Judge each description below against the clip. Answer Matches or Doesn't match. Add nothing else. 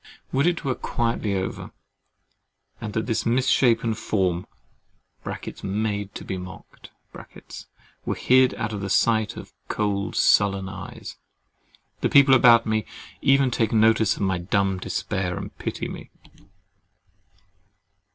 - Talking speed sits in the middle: Doesn't match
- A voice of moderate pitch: Doesn't match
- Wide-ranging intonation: Doesn't match